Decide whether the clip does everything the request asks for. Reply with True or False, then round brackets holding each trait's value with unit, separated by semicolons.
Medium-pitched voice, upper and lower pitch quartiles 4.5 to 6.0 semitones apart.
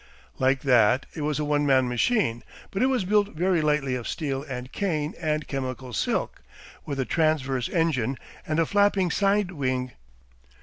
True (150 Hz; 5.0 semitones)